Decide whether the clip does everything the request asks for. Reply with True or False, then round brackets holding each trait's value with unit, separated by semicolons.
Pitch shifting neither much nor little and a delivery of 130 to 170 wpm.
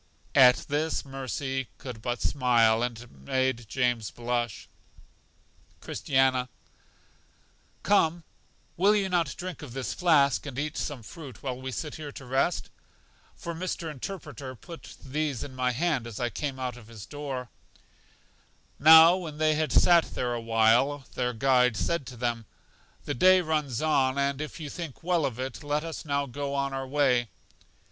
True (3.9 semitones; 165 wpm)